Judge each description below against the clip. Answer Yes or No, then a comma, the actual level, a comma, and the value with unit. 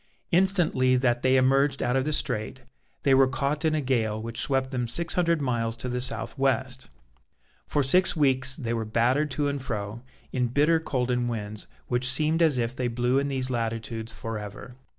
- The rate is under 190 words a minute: No, average, 195 wpm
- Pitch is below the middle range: Yes, low, 130 Hz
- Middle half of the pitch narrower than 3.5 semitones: Yes, average, 3.1 semitones